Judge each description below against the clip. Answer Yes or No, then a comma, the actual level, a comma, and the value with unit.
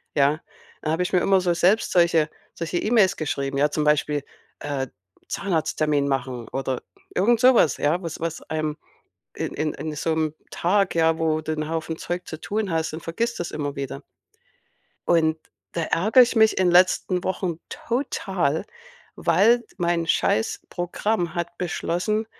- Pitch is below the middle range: No, medium, 165 Hz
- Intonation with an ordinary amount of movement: Yes, average, 3.4 semitones